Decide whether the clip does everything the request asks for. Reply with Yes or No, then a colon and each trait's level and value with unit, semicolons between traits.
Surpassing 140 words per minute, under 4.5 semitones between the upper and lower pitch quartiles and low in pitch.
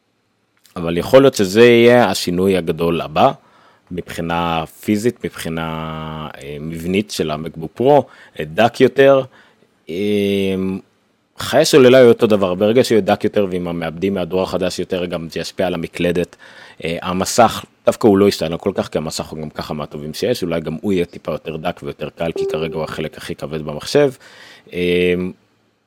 Yes: fast, 150 wpm; average, 4.1 semitones; very low, 90 Hz